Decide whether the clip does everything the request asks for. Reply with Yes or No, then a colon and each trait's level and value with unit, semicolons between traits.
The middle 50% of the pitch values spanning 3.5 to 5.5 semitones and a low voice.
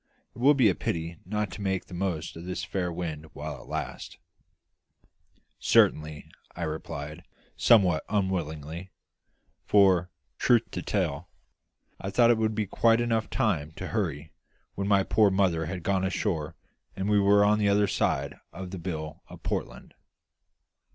Yes: average, 4.0 semitones; very low, 95 Hz